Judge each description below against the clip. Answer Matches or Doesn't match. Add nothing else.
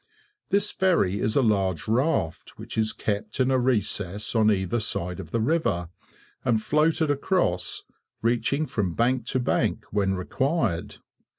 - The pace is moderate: Matches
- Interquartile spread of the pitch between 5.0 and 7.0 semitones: Matches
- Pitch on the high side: Doesn't match